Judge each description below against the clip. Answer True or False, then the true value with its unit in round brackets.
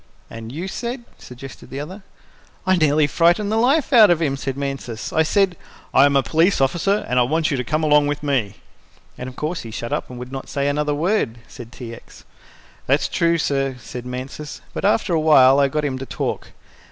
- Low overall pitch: False (145 Hz)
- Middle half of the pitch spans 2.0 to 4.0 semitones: False (4.4 semitones)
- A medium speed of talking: False (215 wpm)